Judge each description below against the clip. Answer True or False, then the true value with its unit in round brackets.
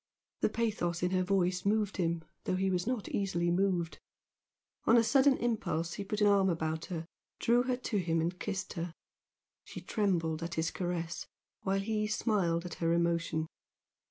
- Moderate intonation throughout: True (3.5 semitones)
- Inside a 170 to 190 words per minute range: True (175 wpm)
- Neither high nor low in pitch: True (180 Hz)